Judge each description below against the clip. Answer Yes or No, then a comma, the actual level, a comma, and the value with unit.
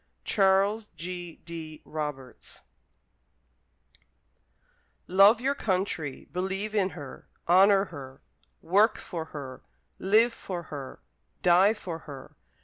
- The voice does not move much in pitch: No, average, 4.2 semitones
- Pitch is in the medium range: Yes, medium, 180 Hz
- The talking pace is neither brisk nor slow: No, slow, 100 wpm